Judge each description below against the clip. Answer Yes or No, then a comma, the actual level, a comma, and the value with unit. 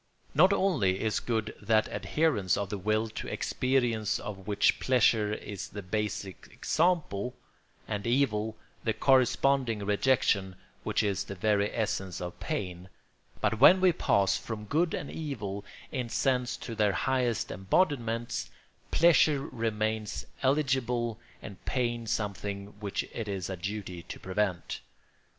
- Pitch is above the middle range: No, low, 110 Hz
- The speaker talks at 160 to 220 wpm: No, slow, 135 wpm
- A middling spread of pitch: Yes, average, 4.1 semitones